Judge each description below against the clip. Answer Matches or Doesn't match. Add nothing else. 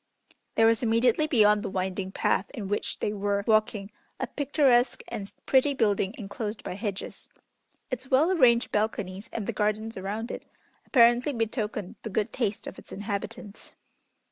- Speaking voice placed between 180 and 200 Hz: Doesn't match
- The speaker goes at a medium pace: Matches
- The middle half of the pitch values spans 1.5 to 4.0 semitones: Matches